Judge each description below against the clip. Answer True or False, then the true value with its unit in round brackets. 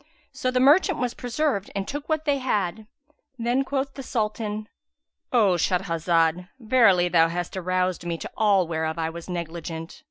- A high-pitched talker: True (195 Hz)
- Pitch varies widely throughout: True (6.7 semitones)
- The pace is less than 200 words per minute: True (160 wpm)